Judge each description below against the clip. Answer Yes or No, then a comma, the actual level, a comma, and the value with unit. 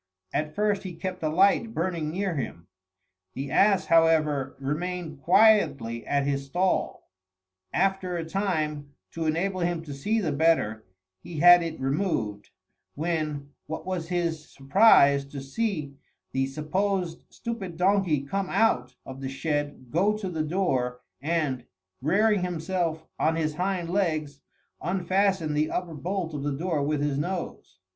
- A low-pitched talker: No, medium, 165 Hz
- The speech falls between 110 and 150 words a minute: Yes, average, 145 wpm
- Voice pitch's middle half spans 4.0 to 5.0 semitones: Yes, average, 4.4 semitones